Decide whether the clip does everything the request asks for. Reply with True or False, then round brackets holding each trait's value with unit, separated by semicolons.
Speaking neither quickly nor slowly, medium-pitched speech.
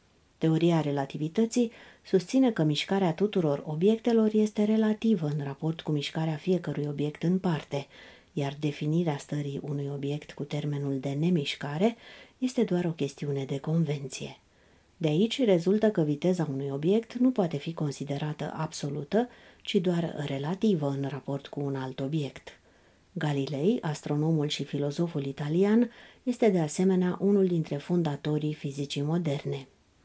True (130 wpm; 155 Hz)